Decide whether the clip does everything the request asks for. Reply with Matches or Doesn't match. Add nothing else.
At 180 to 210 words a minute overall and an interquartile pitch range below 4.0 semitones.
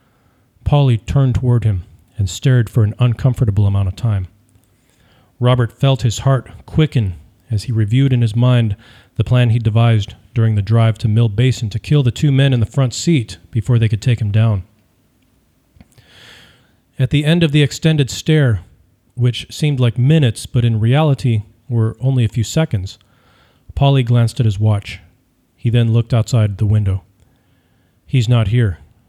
Doesn't match